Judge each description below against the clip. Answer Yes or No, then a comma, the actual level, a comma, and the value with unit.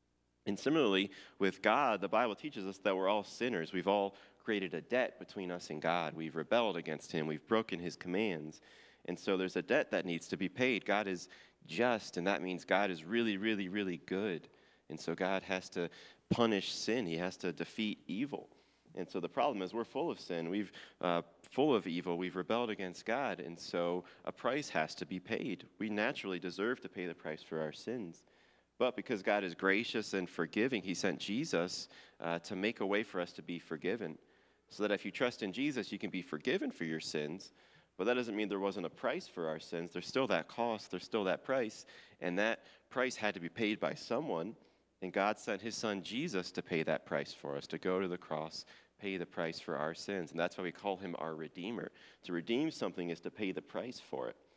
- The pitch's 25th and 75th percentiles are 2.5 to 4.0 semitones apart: Yes, average, 3.4 semitones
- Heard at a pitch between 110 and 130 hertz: No, very low, 95 Hz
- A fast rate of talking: Yes, fast, 220 wpm